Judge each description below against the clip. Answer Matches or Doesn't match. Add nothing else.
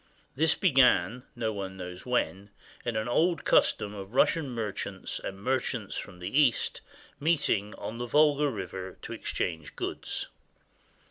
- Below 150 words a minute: Matches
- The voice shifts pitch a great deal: Matches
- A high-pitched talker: Doesn't match